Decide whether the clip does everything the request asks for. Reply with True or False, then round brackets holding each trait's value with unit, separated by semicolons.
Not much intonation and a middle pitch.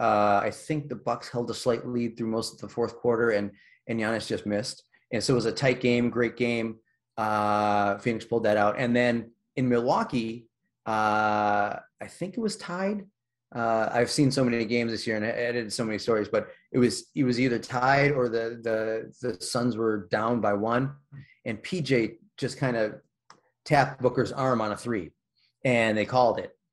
False (2.3 semitones; 120 Hz)